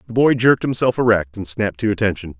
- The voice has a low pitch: Yes, low, 110 Hz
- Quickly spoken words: Yes, fast, 225 wpm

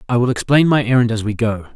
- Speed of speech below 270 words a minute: No, fast, 275 wpm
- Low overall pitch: Yes, low, 120 Hz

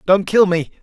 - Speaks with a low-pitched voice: No, high, 190 Hz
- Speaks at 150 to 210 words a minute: No, fast, 220 wpm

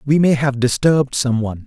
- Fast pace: Yes, fast, 215 wpm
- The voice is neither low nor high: No, low, 130 Hz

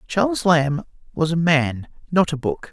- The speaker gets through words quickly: No, average, 175 wpm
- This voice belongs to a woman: No, male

